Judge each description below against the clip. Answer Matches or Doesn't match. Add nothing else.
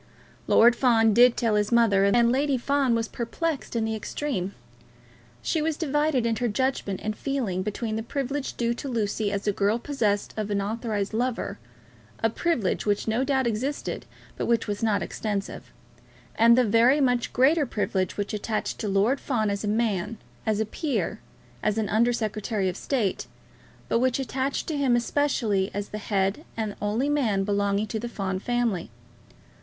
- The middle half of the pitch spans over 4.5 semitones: Doesn't match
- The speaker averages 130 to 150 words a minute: Doesn't match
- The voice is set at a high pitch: Matches